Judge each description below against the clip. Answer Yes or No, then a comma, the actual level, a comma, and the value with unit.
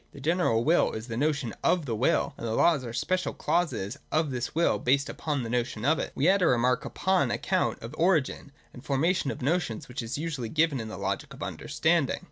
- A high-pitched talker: No, medium, 140 Hz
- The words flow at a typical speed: No, fast, 245 wpm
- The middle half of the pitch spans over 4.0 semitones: Yes, wide, 5.4 semitones